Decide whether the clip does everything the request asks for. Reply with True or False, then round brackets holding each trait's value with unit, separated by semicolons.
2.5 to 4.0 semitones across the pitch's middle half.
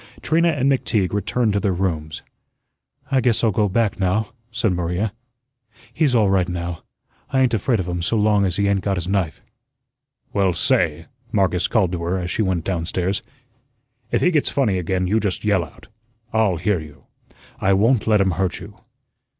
True (3.7 semitones)